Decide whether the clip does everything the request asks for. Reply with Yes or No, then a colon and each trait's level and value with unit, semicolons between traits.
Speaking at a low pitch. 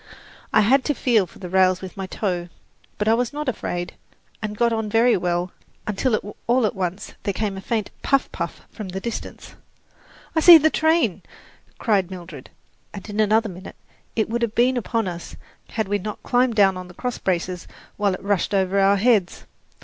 No: high, 205 Hz